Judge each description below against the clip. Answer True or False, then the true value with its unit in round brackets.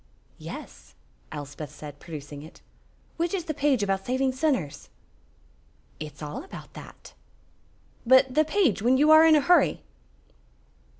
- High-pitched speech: True (260 Hz)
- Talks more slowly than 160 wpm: True (135 wpm)